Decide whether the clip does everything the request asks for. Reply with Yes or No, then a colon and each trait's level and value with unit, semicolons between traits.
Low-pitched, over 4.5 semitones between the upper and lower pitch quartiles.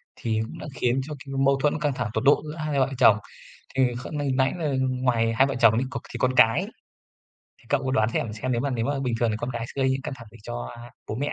No: low, 130 Hz; average, 3.1 semitones